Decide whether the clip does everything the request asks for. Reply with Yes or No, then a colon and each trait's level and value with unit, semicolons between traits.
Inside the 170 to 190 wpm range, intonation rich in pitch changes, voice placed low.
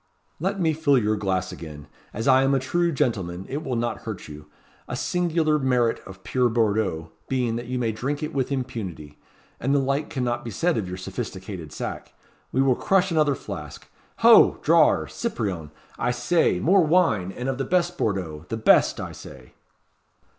Yes: average, 180 wpm; wide, 6.8 semitones; low, 125 Hz